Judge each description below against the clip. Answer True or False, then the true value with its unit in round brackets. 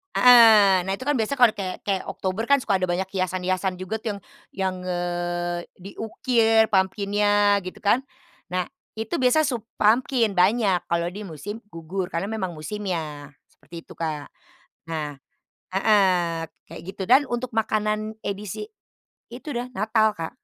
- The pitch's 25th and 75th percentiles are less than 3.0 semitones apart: False (3.7 semitones)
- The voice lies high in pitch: True (200 Hz)